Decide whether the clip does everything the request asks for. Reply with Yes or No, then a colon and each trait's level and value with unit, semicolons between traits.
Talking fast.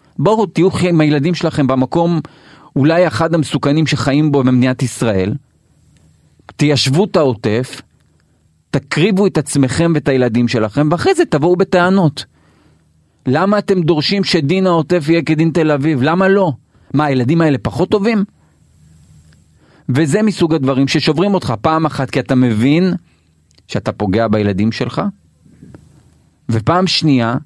No: average, 125 wpm